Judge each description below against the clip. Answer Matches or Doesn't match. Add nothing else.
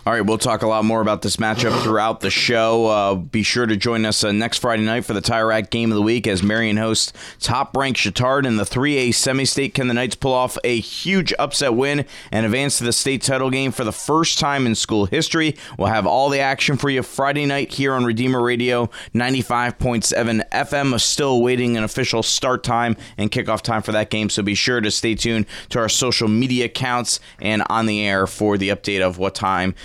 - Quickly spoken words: Matches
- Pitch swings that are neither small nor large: Matches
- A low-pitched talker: Matches